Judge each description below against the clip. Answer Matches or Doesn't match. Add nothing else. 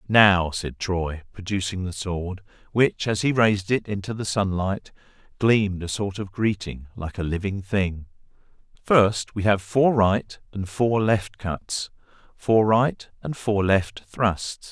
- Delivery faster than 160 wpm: Doesn't match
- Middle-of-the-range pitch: Doesn't match